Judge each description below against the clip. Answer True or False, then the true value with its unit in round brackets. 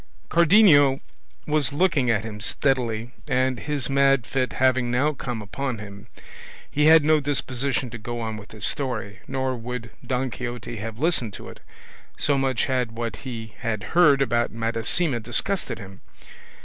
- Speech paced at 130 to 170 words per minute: True (160 wpm)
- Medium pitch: False (125 Hz)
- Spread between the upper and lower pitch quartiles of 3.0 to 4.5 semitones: True (3.4 semitones)